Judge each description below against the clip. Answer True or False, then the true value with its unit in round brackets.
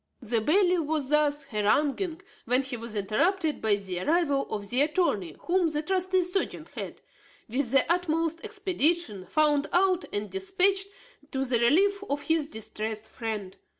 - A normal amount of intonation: False (7.6 semitones)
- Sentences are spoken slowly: False (150 wpm)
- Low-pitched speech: False (300 Hz)